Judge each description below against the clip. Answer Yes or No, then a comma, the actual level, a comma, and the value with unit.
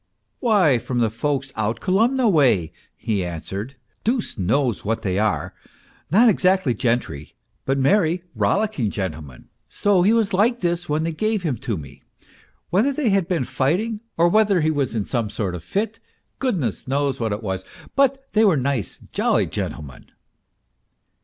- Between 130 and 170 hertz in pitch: Yes, medium, 140 Hz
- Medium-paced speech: Yes, average, 165 wpm